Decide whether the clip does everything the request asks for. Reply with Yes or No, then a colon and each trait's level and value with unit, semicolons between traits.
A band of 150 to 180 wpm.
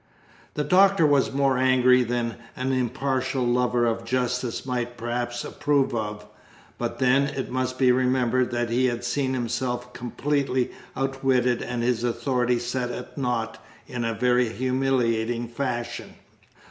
No: average, 140 wpm